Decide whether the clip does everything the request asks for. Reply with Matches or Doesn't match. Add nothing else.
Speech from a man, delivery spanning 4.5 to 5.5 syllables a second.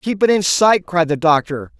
Matches